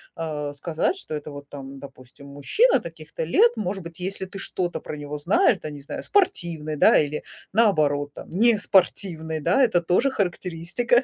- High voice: No, medium, 170 Hz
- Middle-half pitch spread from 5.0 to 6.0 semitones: Yes, average, 5.3 semitones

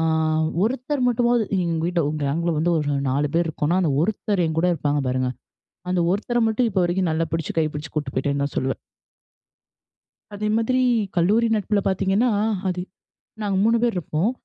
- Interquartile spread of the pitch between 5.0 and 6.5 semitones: Yes, wide, 5.6 semitones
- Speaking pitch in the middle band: Yes, medium, 175 Hz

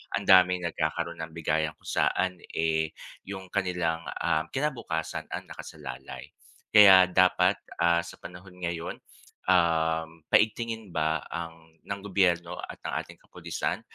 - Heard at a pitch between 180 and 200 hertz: No, very low, 85 Hz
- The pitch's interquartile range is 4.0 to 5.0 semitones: No, narrow, 2.4 semitones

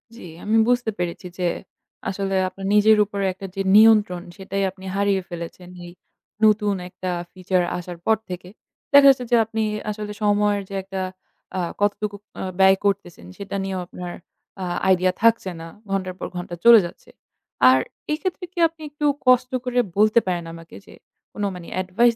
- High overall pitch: Yes, high, 200 Hz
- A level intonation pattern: No, average, 3.2 semitones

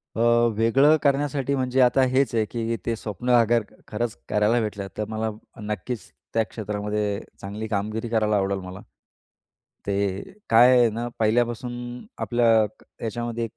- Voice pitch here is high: No, low, 115 Hz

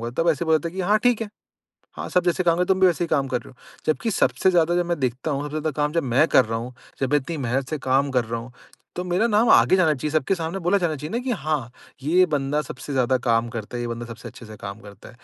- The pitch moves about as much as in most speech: No, wide, 6.0 semitones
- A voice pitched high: No, medium, 150 Hz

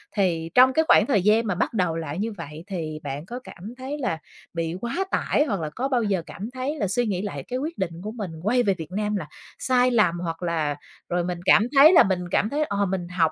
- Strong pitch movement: Yes, wide, 6.0 semitones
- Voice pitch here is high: Yes, high, 200 Hz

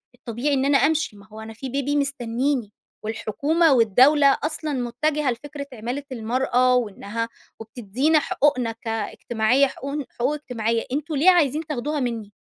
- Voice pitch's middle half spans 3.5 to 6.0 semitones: Yes, average, 4.1 semitones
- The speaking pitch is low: No, very high, 255 Hz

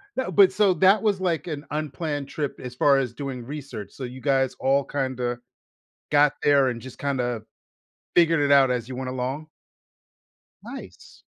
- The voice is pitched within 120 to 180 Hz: Yes, medium, 140 Hz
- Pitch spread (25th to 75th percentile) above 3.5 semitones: No, average, 3.1 semitones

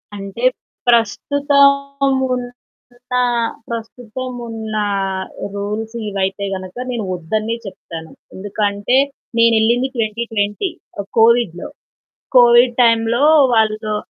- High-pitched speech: Yes, high, 225 Hz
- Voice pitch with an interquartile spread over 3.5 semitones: No, average, 2.7 semitones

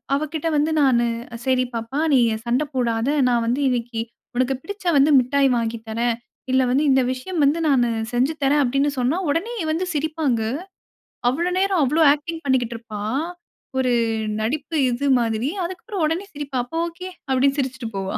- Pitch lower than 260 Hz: No, very high, 270 Hz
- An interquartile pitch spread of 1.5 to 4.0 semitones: No, average, 4.5 semitones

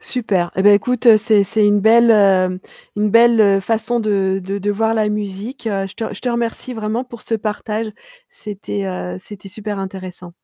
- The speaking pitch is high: Yes, high, 210 Hz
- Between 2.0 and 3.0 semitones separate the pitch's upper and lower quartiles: Yes, narrow, 2.6 semitones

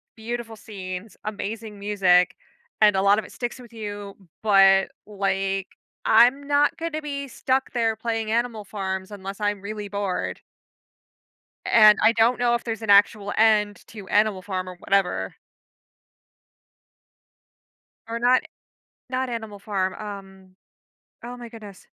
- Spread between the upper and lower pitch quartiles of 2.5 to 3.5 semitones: Yes, average, 2.8 semitones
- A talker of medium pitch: No, high, 210 Hz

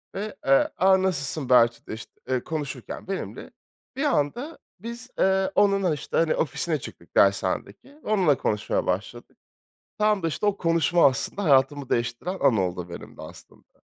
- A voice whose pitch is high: No, medium, 155 Hz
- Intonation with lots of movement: Yes, wide, 7.7 semitones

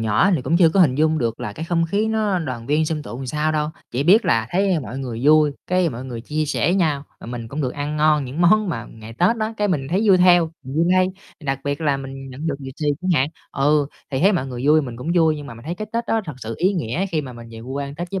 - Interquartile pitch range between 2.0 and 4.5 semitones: No, average, 4.9 semitones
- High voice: No, medium, 150 Hz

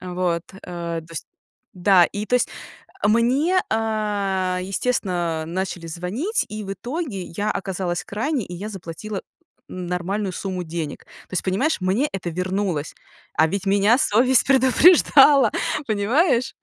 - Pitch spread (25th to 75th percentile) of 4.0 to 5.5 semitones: Yes, average, 4.7 semitones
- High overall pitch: Yes, high, 195 Hz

